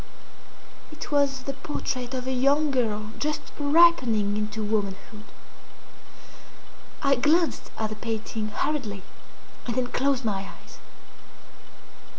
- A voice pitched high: Yes, very high, 250 Hz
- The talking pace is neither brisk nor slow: No, slow, 115 wpm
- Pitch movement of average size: Yes, average, 4.8 semitones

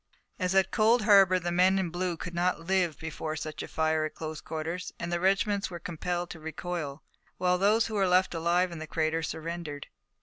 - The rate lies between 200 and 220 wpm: Yes, fast, 205 wpm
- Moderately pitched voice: Yes, medium, 175 Hz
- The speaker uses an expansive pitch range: No, narrow, 2.5 semitones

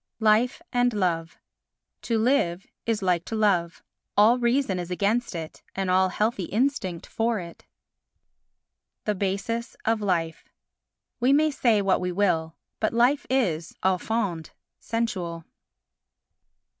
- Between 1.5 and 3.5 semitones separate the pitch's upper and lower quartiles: No, average, 4.7 semitones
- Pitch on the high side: Yes, high, 205 Hz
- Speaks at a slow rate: Yes, slow, 125 wpm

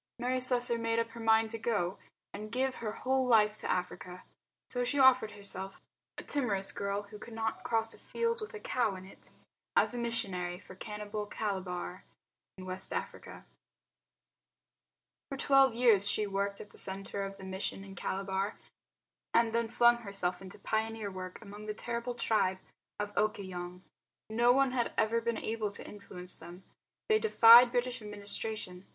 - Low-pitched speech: No, high, 215 Hz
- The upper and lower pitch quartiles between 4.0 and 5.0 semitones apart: No, average, 3.4 semitones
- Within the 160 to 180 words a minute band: Yes, average, 170 wpm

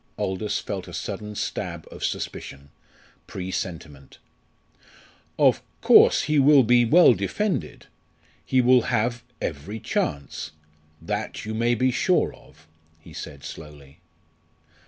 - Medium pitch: No, low, 105 Hz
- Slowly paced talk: Yes, slow, 115 wpm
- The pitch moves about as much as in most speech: No, wide, 8.1 semitones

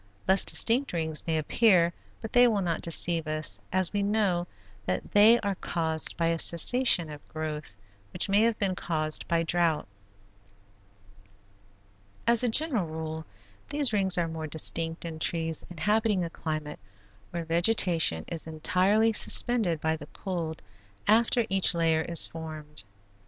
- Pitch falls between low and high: Yes, medium, 170 Hz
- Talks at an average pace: Yes, average, 145 wpm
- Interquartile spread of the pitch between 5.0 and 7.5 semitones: No, average, 4.4 semitones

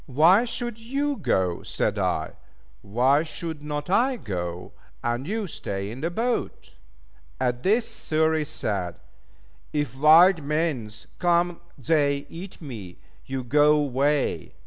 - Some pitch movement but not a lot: No, wide, 6.0 semitones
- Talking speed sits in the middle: No, slow, 125 wpm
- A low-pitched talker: No, medium, 150 Hz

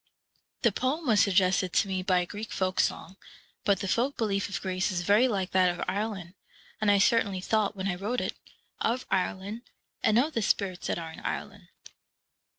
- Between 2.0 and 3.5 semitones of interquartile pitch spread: Yes, average, 2.9 semitones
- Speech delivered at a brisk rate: No, average, 195 wpm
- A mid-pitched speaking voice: No, high, 200 Hz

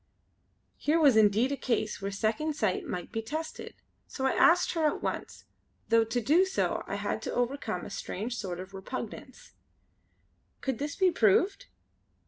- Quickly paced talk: No, average, 165 wpm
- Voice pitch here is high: Yes, high, 240 Hz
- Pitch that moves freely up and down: Yes, wide, 5.8 semitones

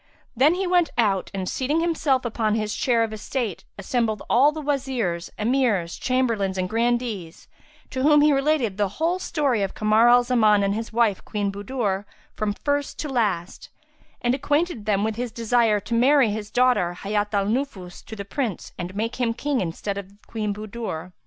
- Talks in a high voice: Yes, high, 225 Hz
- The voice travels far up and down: No, average, 4.3 semitones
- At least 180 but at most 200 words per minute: Yes, average, 185 wpm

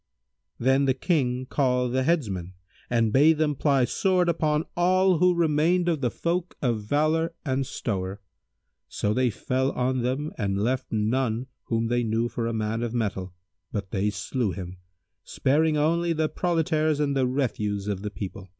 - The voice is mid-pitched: No, low, 130 Hz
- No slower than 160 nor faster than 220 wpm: Yes, average, 170 wpm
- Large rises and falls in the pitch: Yes, wide, 5.8 semitones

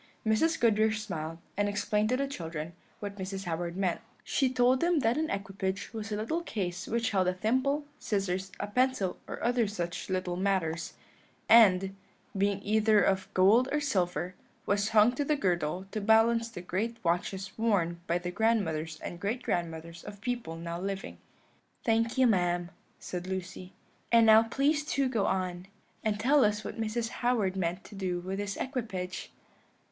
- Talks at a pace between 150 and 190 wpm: Yes, average, 170 wpm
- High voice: Yes, high, 200 Hz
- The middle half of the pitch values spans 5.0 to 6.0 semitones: No, average, 4.1 semitones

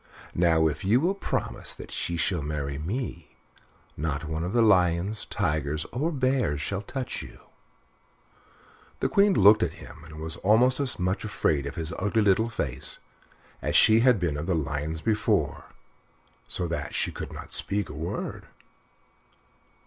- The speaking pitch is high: No, very low, 90 Hz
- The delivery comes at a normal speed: Yes, average, 160 wpm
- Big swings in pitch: Yes, wide, 6.0 semitones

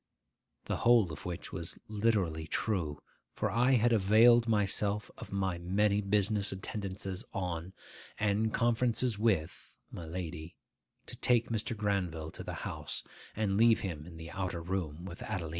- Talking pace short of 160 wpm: Yes, average, 150 wpm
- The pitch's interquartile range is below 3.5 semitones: No, average, 3.9 semitones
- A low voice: Yes, low, 100 Hz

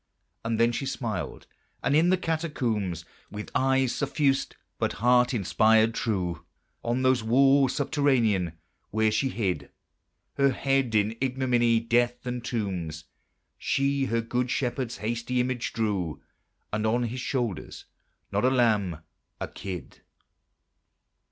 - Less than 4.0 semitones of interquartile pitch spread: Yes, average, 3.6 semitones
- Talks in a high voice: No, low, 120 Hz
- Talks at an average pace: No, slow, 125 wpm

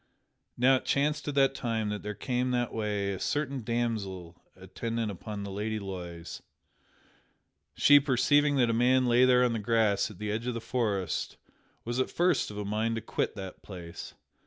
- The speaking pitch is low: Yes, low, 115 Hz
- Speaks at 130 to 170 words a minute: No, average, 185 wpm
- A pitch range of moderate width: Yes, average, 3.8 semitones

